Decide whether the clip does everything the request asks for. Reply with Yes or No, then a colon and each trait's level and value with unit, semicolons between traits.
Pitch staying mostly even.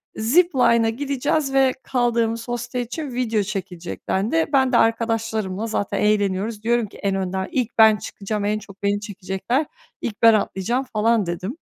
No: average, 3.3 semitones